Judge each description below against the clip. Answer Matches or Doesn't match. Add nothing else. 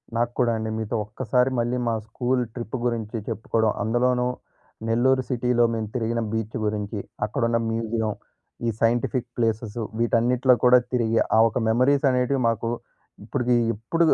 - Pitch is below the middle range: Matches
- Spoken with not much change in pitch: Matches